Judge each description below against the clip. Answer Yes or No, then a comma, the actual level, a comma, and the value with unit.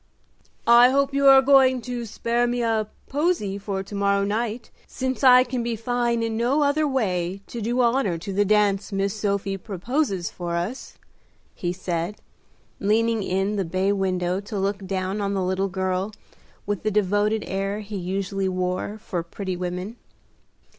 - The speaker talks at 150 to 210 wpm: Yes, average, 165 wpm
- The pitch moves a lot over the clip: No, average, 3.8 semitones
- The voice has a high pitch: Yes, high, 205 Hz